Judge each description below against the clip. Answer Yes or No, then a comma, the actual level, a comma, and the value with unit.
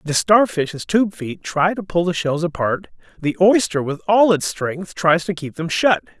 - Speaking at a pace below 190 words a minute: No, fast, 205 wpm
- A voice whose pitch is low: No, medium, 175 Hz